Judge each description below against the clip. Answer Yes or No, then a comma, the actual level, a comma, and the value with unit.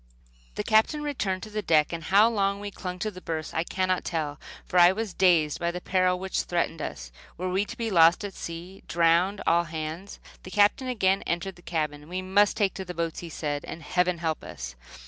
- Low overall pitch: No, medium, 180 Hz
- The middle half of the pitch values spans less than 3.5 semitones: Yes, average, 3.1 semitones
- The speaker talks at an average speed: No, fast, 220 wpm